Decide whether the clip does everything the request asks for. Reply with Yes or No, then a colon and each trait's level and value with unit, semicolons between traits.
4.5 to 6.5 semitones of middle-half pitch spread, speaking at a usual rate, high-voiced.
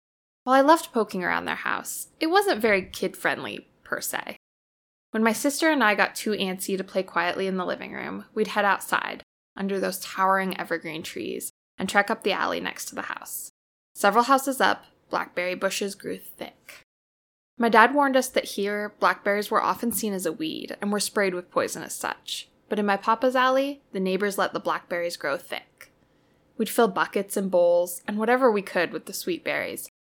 No: average, 4.1 semitones; average, 195 wpm; high, 205 Hz